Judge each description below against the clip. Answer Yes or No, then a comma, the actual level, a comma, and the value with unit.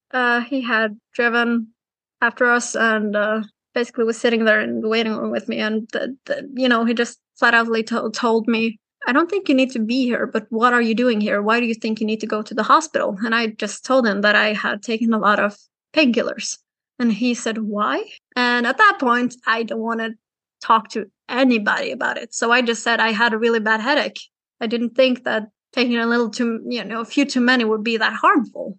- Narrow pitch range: Yes, narrow, 1.8 semitones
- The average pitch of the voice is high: Yes, high, 235 Hz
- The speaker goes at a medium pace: No, fast, 235 wpm